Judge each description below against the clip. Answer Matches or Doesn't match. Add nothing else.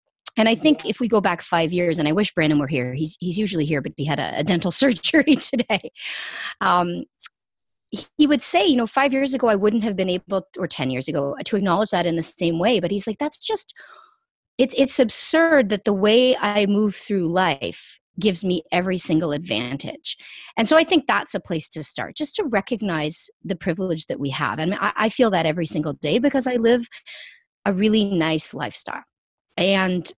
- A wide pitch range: Matches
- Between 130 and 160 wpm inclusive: Doesn't match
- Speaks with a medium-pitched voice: Doesn't match